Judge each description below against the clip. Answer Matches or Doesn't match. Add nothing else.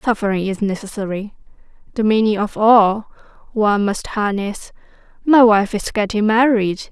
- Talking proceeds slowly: Matches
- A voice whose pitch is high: Matches